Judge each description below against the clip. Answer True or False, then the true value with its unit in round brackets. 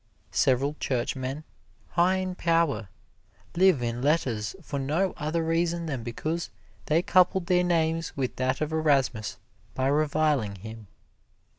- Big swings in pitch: False (4.5 semitones)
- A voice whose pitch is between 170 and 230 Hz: False (150 Hz)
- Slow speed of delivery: True (130 wpm)